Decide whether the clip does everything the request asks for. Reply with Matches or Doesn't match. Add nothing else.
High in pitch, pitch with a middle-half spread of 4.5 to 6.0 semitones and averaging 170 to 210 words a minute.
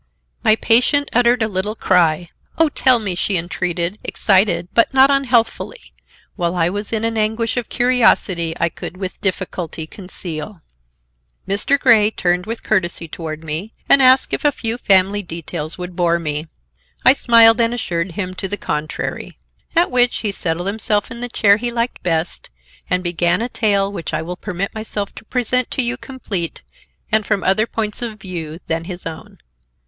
Matches